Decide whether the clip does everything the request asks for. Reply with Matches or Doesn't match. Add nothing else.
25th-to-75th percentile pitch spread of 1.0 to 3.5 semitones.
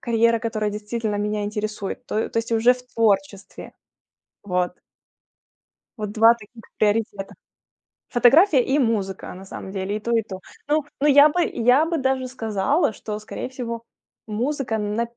Matches